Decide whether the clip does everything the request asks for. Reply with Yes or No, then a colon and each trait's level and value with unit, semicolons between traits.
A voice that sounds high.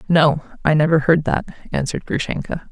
No: medium, 155 Hz